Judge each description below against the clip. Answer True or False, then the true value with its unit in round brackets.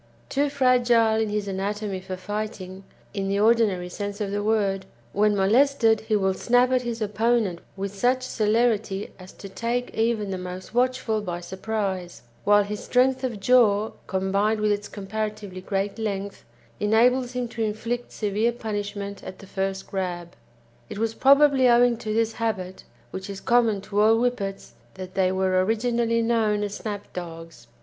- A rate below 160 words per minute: False (165 wpm)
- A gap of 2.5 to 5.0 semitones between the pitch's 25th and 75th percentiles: True (3.1 semitones)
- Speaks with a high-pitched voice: True (210 Hz)